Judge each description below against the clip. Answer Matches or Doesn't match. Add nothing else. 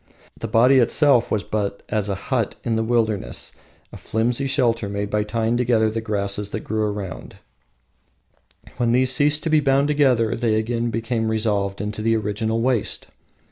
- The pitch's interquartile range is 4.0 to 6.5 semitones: Doesn't match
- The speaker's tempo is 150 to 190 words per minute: Matches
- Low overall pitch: Matches